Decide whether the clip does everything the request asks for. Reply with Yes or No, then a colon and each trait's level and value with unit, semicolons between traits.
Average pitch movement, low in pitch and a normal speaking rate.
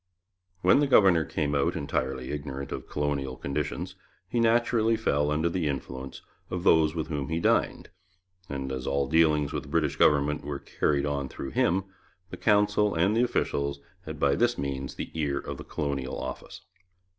Yes: average, 3.9 semitones; very low, 75 Hz; average, 175 wpm